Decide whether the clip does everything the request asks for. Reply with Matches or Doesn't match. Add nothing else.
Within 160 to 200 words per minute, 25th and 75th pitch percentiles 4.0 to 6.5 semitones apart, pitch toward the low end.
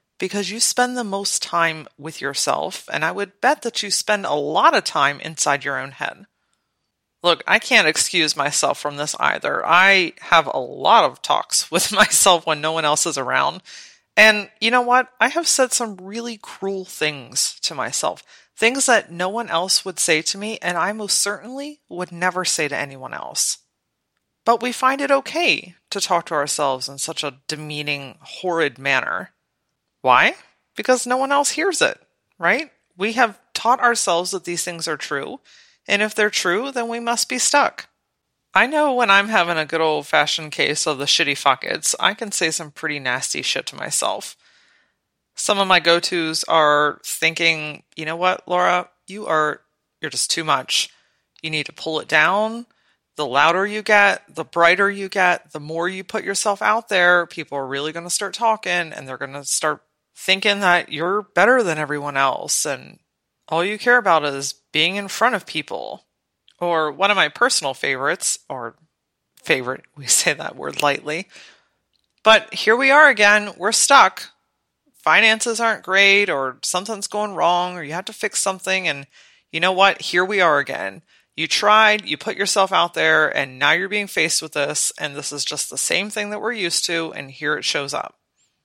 Doesn't match